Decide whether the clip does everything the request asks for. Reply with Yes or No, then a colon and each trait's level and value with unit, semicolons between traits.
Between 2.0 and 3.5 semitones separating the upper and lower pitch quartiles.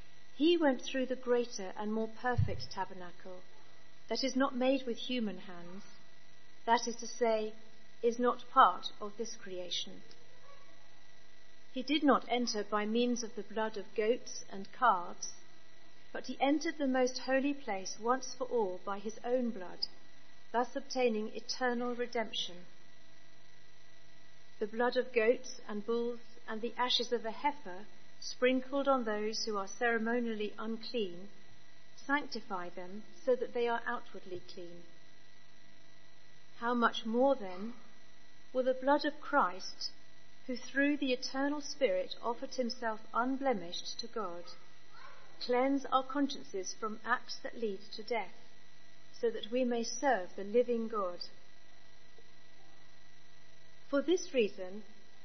No: average, 4.5 semitones